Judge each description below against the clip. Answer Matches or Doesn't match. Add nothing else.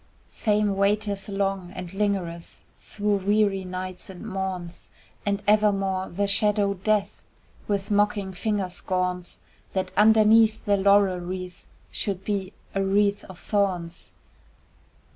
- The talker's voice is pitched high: Matches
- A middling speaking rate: Doesn't match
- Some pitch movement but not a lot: Doesn't match